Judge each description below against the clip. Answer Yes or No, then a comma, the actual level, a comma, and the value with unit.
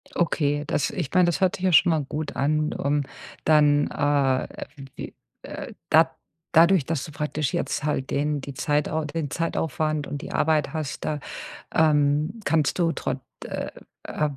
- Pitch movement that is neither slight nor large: No, narrow, 1.9 semitones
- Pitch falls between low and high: Yes, medium, 150 Hz